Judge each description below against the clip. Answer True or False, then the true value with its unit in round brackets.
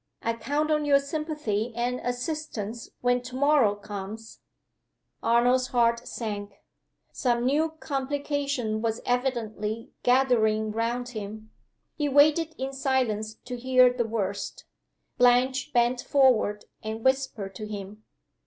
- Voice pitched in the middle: False (245 Hz)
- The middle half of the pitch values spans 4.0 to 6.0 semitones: False (3.6 semitones)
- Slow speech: True (120 wpm)